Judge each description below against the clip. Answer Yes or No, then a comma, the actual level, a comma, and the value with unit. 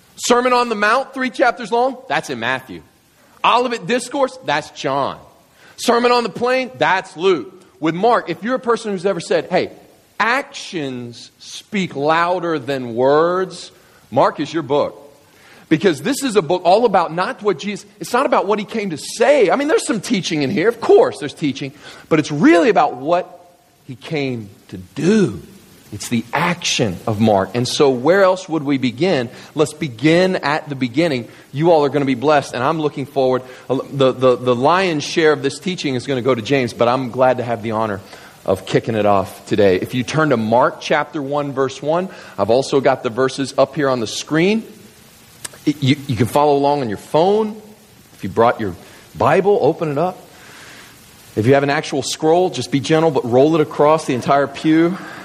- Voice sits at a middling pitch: Yes, medium, 155 Hz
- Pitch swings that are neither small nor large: No, wide, 6.2 semitones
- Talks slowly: No, average, 200 wpm